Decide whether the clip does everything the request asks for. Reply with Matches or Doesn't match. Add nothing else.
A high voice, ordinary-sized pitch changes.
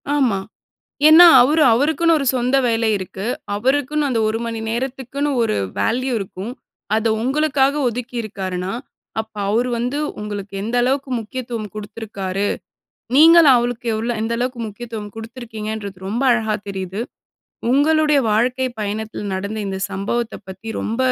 Matches